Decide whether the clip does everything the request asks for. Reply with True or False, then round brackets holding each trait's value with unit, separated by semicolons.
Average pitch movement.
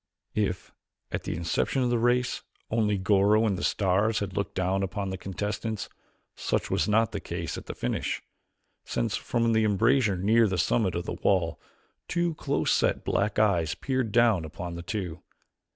True (3.6 semitones)